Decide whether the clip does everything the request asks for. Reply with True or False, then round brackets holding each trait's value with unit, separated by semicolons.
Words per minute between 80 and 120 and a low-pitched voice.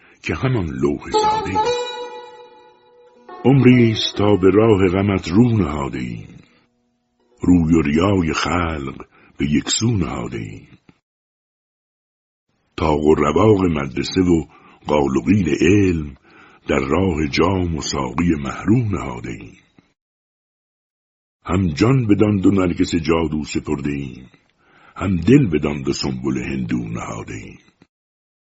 True (110 wpm; 95 Hz)